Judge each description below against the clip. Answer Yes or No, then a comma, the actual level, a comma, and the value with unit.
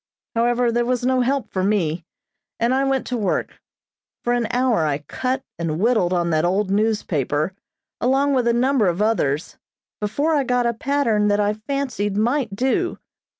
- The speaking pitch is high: Yes, high, 230 Hz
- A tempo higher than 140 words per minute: Yes, average, 175 wpm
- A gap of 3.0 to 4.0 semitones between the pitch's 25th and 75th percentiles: No, average, 4.6 semitones